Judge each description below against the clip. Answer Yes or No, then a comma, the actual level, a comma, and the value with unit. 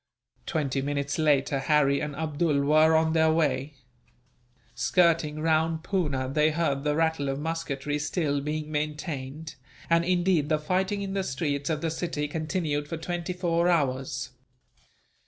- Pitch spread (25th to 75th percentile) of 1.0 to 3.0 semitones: Yes, narrow, 2.5 semitones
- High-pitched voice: No, medium, 155 Hz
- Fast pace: No, average, 145 wpm